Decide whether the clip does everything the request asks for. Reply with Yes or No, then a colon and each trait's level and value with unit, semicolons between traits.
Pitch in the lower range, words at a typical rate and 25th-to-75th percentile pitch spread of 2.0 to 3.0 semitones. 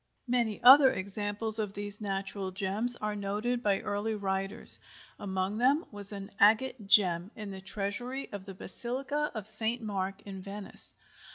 No: high, 205 Hz; average, 155 wpm; narrow, 2.6 semitones